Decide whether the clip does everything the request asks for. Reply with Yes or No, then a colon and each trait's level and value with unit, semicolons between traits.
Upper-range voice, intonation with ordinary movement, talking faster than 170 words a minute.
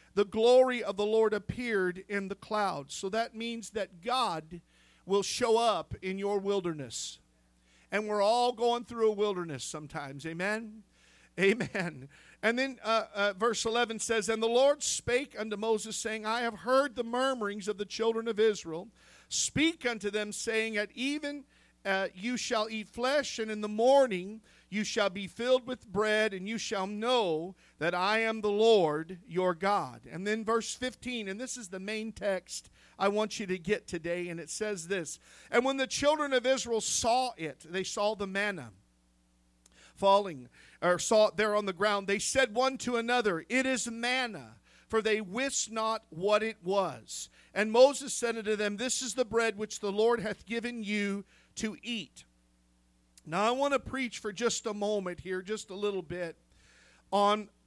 Yes: high, 210 Hz; average, 3.6 semitones; average, 180 wpm